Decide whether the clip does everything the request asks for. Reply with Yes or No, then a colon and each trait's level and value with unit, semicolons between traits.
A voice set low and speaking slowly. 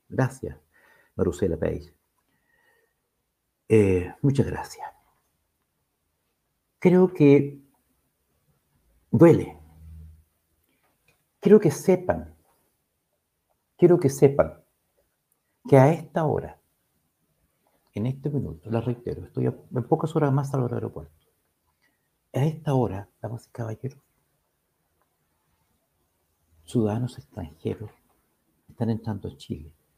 Yes: low, 115 Hz; slow, 85 wpm